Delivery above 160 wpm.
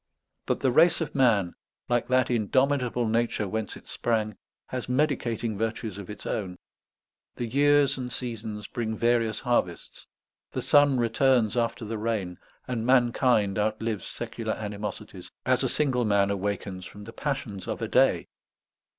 No: average, 150 wpm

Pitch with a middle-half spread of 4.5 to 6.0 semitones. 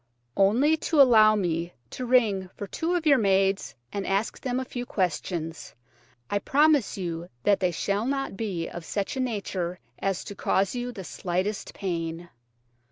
Yes: average, 5.3 semitones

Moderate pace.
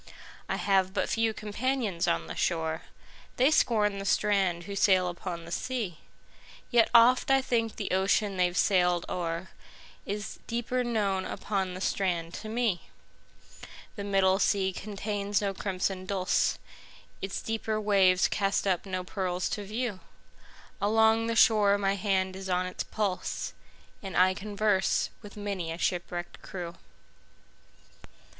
No: slow, 125 wpm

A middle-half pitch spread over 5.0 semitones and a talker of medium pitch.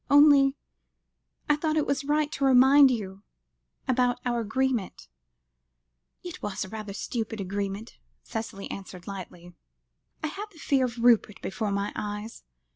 No: wide, 5.4 semitones; high, 235 Hz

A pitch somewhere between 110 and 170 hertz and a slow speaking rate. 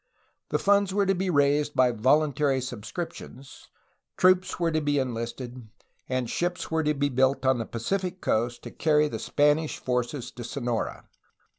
No: medium, 140 Hz; average, 165 wpm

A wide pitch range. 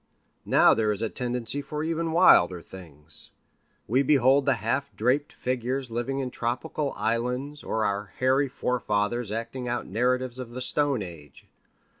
No: average, 3.5 semitones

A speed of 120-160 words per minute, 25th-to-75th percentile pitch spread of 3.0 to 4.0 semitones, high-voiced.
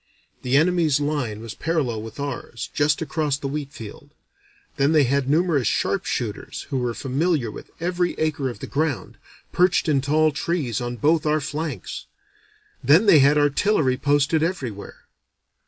No: average, 155 wpm; average, 3.4 semitones; medium, 145 Hz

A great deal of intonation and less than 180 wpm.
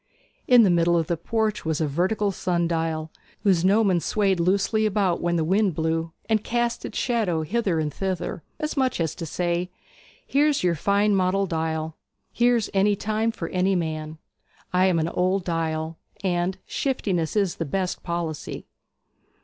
No: average, 3.9 semitones; average, 165 wpm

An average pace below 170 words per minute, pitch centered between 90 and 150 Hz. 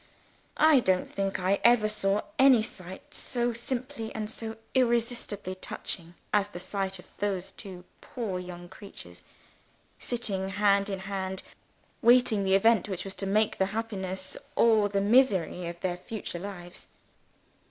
No: average, 140 wpm; high, 200 Hz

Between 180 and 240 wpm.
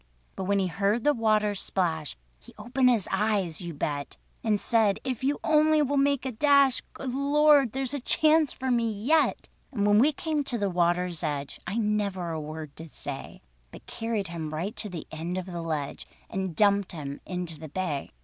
Yes: average, 195 wpm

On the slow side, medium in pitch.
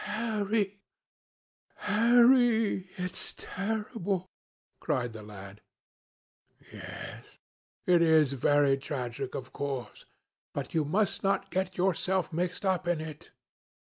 Yes: slow, 110 wpm; medium, 180 Hz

